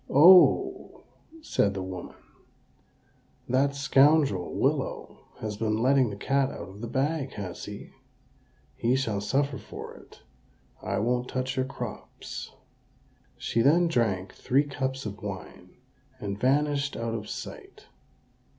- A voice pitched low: Yes, low, 130 Hz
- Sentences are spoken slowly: Yes, slow, 130 wpm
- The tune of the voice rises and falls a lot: No, average, 5.0 semitones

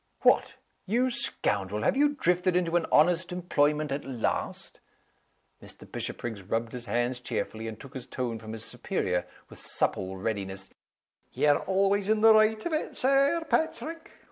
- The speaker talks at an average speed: Yes, average, 155 wpm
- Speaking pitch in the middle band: Yes, medium, 150 Hz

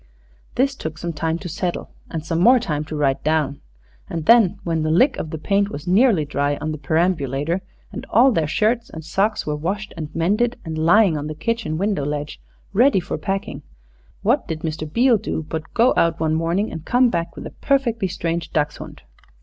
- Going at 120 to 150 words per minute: No, average, 200 wpm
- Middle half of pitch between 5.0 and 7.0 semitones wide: Yes, average, 5.3 semitones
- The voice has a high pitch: No, medium, 170 Hz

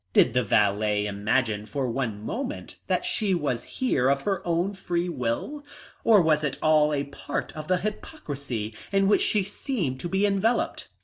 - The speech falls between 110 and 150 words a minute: No, average, 175 wpm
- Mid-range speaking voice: Yes, medium, 150 Hz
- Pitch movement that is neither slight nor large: No, wide, 7.9 semitones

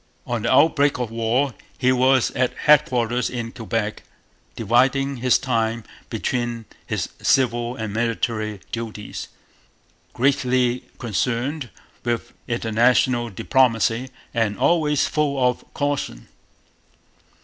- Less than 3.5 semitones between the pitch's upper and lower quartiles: Yes, narrow, 2.4 semitones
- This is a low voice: Yes, low, 120 Hz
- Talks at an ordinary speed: No, slow, 105 wpm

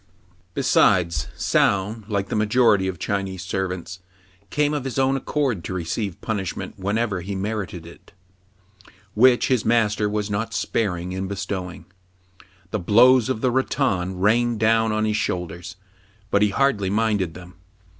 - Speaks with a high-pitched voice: No, low, 105 Hz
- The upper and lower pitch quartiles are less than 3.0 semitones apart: No, average, 3.3 semitones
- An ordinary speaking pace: Yes, average, 150 wpm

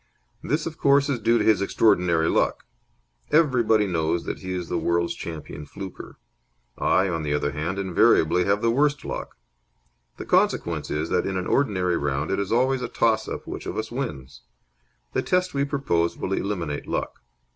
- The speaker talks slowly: No, average, 180 wpm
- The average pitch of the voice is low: Yes, very low, 95 Hz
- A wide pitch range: Yes, wide, 6.3 semitones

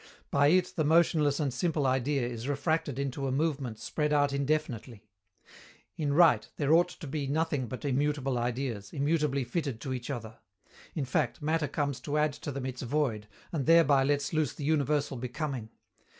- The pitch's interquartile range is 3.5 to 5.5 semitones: No, average, 2.8 semitones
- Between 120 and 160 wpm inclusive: No, average, 175 wpm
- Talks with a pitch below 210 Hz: Yes, medium, 140 Hz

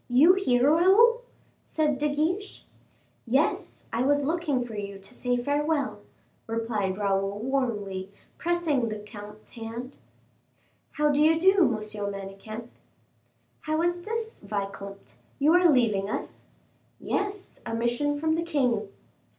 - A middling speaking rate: No, slow, 130 wpm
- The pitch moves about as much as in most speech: No, wide, 6.9 semitones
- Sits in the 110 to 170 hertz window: No, very high, 255 Hz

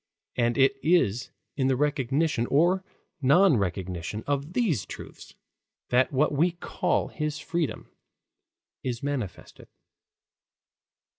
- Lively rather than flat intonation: No, average, 4.4 semitones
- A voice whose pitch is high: No, medium, 140 Hz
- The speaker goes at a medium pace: No, slow, 105 wpm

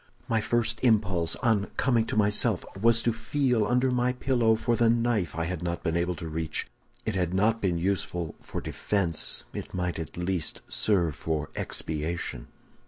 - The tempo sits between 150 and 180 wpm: Yes, average, 175 wpm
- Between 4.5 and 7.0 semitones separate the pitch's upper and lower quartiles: Yes, average, 5.2 semitones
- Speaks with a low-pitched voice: Yes, low, 100 Hz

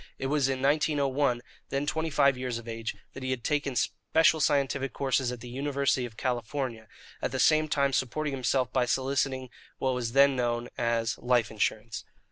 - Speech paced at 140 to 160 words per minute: No, average, 180 wpm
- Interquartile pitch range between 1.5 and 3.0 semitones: Yes, narrow, 2.5 semitones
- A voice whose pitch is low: Yes, low, 130 Hz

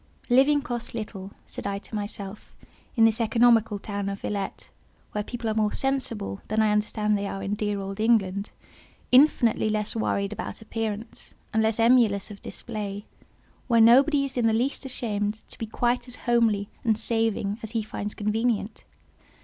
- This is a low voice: No, high, 220 Hz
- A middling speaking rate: Yes, average, 165 wpm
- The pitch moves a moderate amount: No, narrow, 2.3 semitones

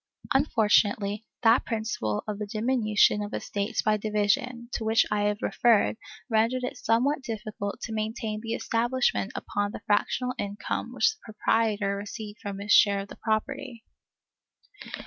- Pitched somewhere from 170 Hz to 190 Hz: No, high, 215 Hz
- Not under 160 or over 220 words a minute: No, average, 145 wpm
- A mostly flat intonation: Yes, narrow, 2.3 semitones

